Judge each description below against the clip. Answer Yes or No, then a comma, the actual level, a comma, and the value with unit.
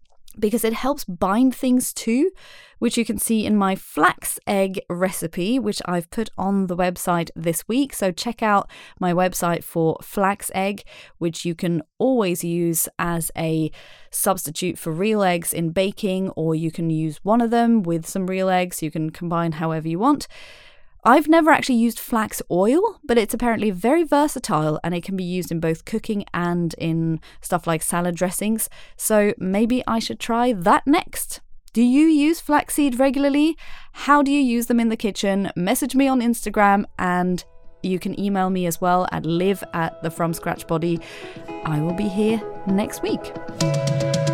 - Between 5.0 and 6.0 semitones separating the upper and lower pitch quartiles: Yes, wide, 5.5 semitones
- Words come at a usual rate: Yes, average, 175 wpm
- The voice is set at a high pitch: Yes, high, 195 Hz